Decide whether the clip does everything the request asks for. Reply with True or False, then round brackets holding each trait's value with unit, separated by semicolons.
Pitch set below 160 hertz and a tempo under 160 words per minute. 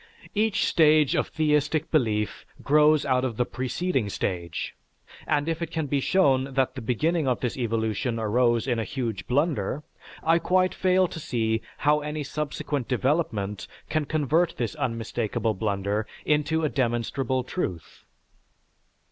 True (135 Hz; 145 wpm)